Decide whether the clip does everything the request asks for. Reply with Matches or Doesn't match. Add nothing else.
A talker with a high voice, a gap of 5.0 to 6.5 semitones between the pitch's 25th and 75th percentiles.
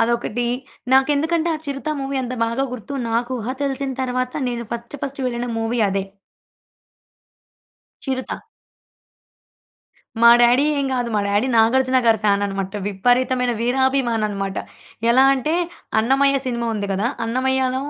Doesn't match